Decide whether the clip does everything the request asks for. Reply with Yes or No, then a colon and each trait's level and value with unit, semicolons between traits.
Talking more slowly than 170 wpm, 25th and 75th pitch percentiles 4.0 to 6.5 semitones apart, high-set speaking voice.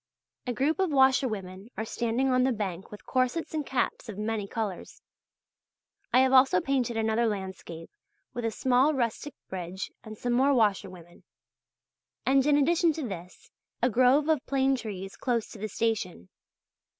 Yes: average, 160 wpm; average, 4.6 semitones; high, 235 Hz